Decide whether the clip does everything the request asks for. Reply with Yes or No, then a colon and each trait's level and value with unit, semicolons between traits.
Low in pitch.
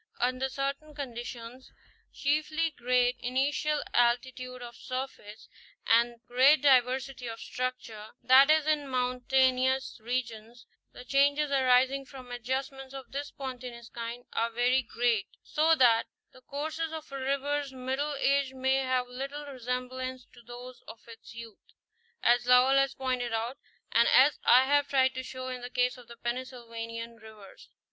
No: very high, 255 Hz